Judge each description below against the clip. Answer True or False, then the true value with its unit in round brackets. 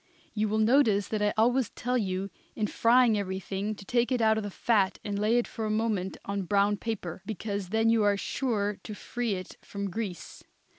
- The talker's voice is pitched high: True (210 Hz)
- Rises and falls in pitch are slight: True (2.2 semitones)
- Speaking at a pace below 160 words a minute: False (205 wpm)